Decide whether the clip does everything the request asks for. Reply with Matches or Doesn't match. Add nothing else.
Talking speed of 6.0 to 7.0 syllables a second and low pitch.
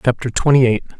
Matches